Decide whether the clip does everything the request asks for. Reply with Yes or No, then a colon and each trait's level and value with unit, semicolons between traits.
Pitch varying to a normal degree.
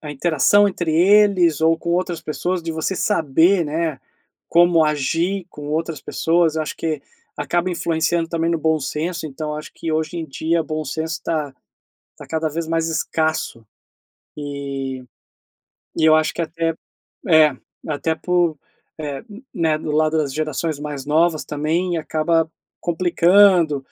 No: narrow, 1.9 semitones